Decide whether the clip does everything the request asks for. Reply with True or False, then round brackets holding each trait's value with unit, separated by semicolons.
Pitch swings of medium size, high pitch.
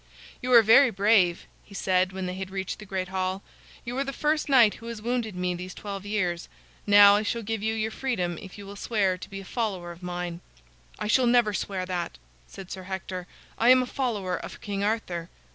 True (3.5 semitones; 200 Hz)